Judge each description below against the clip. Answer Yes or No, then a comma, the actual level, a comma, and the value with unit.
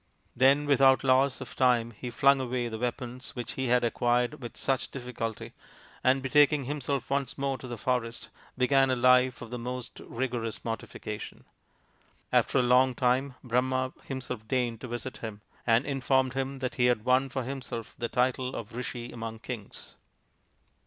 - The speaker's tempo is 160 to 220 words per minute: Yes, average, 165 wpm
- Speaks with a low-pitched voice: Yes, low, 125 Hz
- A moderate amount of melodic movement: No, narrow, 1.7 semitones